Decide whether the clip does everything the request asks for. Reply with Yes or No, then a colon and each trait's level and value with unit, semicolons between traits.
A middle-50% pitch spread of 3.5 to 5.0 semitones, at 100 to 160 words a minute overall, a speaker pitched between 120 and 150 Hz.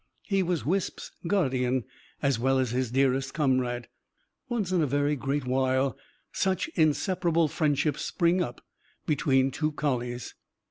Yes: average, 4.2 semitones; slow, 135 wpm; medium, 140 Hz